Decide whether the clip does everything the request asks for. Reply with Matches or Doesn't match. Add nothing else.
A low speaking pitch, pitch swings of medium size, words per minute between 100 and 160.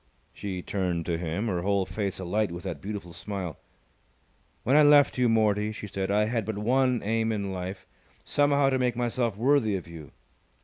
Doesn't match